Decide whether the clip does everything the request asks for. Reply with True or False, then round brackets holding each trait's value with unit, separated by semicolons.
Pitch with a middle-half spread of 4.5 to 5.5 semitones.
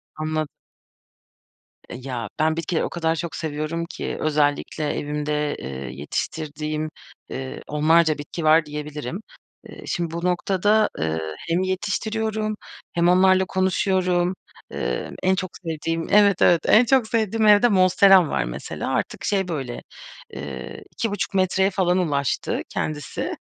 False (4.0 semitones)